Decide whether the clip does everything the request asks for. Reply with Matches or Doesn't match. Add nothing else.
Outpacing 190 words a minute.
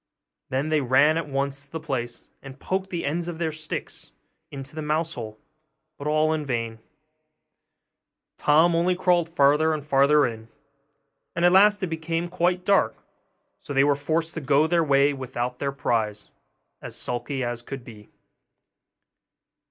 Doesn't match